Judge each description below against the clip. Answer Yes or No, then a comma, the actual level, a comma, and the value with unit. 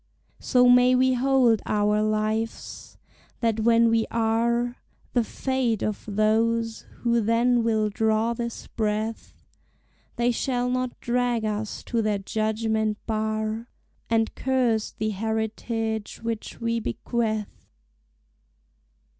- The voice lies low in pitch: No, high, 225 Hz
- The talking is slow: Yes, slow, 115 wpm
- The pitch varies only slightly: Yes, narrow, 1.6 semitones